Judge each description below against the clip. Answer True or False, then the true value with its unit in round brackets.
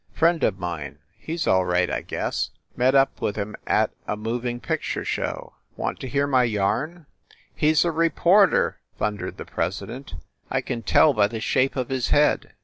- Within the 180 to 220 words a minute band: True (190 wpm)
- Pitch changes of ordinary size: False (6.3 semitones)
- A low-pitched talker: True (125 Hz)